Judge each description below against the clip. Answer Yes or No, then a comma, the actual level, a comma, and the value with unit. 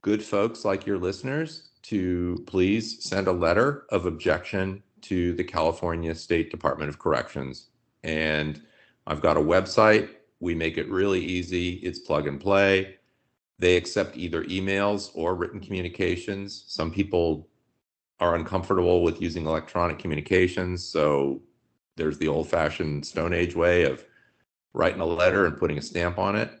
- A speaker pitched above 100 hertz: No, very low, 90 Hz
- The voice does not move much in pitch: No, average, 3.0 semitones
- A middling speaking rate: Yes, average, 150 wpm